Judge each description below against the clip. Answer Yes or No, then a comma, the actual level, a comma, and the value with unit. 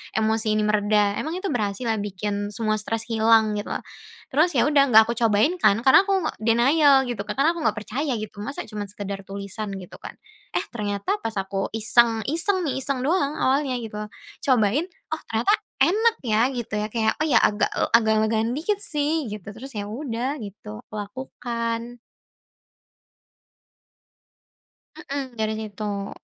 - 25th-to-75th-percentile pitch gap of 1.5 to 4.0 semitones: No, average, 4.7 semitones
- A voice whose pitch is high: Yes, high, 225 Hz